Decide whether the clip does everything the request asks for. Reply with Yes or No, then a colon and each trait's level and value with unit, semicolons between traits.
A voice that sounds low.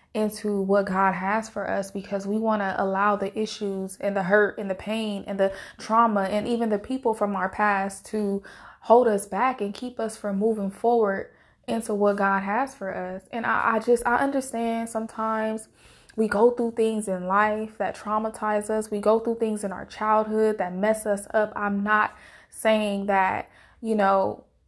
No: high, 210 Hz